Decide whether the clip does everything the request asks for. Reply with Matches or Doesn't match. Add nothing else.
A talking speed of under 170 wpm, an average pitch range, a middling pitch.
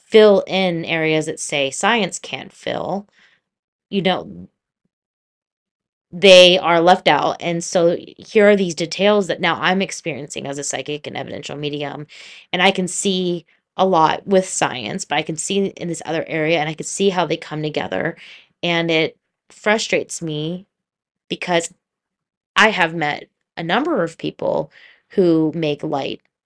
Matches